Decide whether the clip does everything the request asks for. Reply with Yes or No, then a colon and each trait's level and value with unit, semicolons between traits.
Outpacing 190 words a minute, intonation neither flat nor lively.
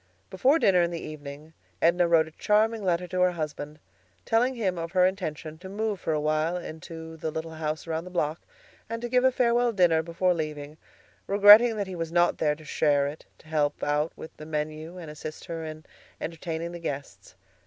Yes: fast, 205 wpm; average, 3.2 semitones